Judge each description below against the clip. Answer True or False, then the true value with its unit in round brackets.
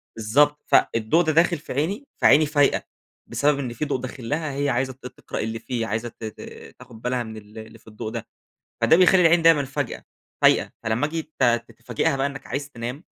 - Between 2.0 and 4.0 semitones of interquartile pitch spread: False (4.6 semitones)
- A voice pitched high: False (135 Hz)